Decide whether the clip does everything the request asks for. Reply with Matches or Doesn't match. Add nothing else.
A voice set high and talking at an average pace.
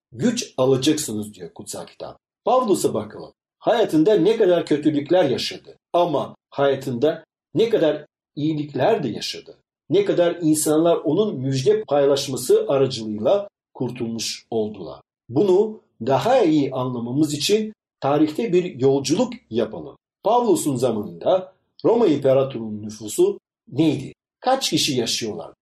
Doesn't match